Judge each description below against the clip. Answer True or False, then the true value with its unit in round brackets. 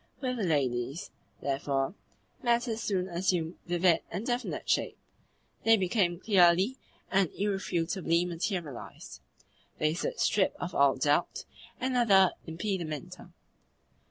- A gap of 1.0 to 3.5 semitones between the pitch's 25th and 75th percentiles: False (4.0 semitones)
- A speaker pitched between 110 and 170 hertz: False (180 Hz)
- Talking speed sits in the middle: False (110 wpm)